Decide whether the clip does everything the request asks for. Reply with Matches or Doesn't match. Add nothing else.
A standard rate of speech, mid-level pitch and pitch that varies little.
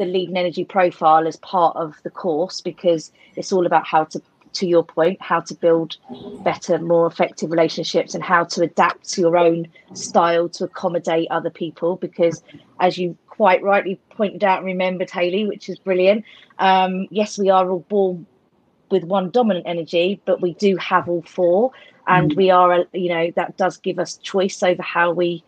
Matches